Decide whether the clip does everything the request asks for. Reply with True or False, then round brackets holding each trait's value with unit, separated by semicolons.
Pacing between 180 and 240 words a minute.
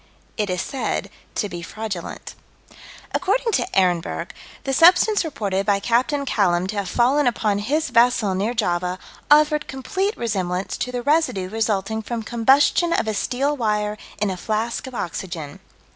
False (155 wpm)